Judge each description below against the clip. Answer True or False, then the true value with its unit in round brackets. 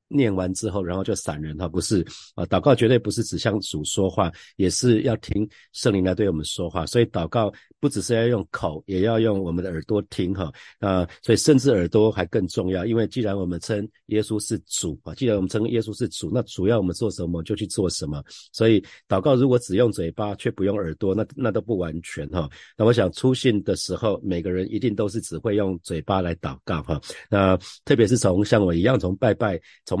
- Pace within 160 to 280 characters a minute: False (325 characters per minute)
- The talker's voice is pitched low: True (100 Hz)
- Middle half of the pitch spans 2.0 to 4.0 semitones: True (3.7 semitones)